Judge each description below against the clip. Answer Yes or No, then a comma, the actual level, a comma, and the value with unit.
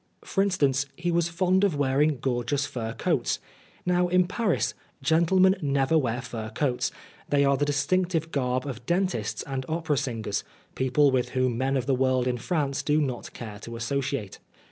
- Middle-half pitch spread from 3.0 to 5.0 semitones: Yes, average, 4.6 semitones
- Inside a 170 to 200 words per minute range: Yes, average, 175 wpm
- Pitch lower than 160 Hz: Yes, medium, 140 Hz